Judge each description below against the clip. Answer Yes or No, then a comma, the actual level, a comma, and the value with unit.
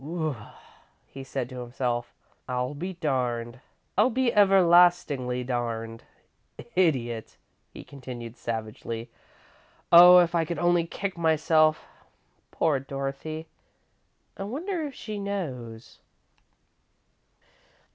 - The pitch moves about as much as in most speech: No, wide, 6.2 semitones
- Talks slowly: Yes, slow, 100 wpm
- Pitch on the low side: No, medium, 145 Hz